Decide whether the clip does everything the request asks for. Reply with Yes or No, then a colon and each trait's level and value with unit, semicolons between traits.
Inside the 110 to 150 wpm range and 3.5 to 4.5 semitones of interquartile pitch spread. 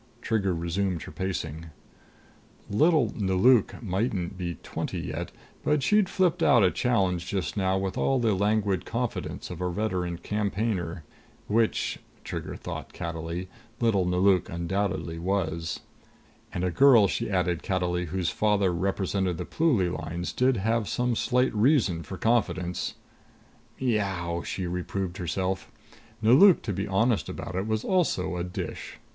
Yes: average, 140 wpm; average, 3.9 semitones